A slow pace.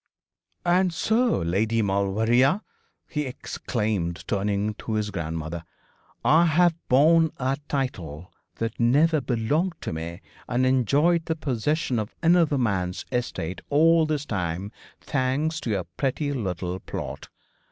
Yes: slow, 125 wpm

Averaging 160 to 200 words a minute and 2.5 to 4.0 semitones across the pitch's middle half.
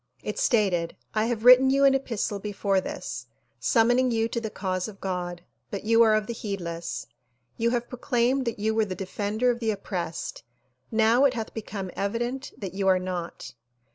Yes: average, 185 wpm; average, 3.7 semitones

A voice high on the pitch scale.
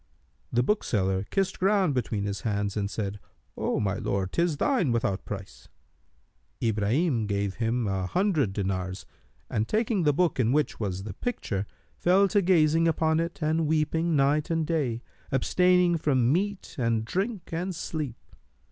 No: medium, 140 Hz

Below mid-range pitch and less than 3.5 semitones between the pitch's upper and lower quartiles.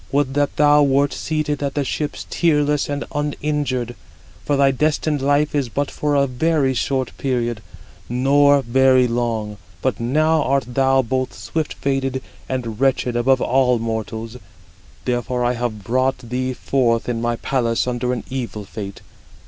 Yes: low, 130 Hz; average, 2.9 semitones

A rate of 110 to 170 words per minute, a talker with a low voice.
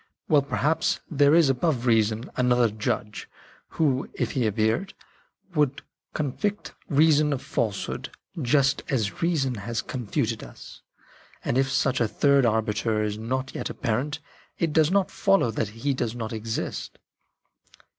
Yes: average, 145 wpm; low, 130 Hz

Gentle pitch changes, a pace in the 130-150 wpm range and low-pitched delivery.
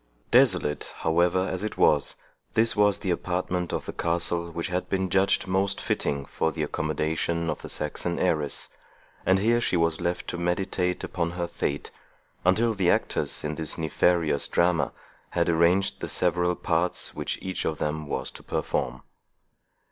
No: narrow, 2.3 semitones; average, 165 wpm; very low, 85 Hz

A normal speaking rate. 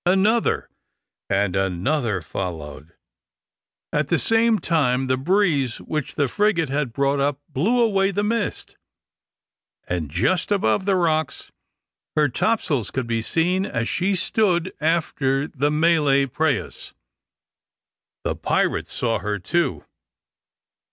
No: slow, 120 wpm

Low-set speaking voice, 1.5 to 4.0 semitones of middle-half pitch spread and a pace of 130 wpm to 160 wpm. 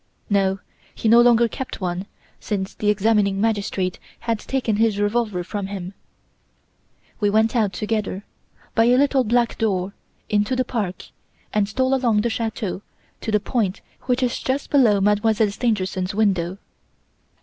No: high, 210 Hz; average, 2.9 semitones; average, 150 wpm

